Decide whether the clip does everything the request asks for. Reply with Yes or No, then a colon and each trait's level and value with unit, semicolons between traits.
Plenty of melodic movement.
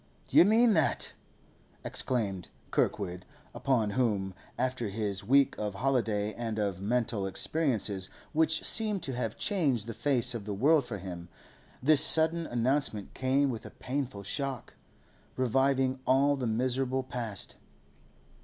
No: average, 4.9 semitones